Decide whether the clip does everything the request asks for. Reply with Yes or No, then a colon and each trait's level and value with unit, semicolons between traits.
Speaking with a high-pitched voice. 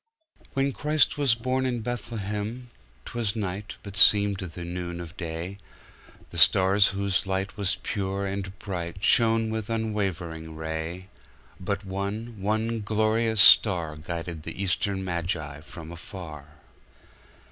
No: low, 100 Hz